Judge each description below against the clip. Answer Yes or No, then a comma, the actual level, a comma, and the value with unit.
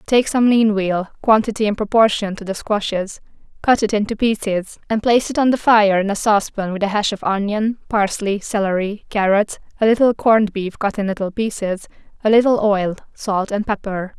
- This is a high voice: Yes, high, 210 Hz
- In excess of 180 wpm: Yes, average, 190 wpm